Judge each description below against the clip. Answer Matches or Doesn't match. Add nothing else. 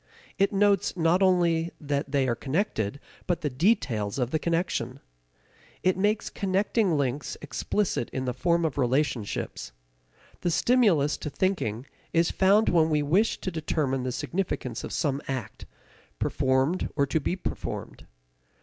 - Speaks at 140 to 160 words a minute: Matches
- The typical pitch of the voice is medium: Matches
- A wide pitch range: Matches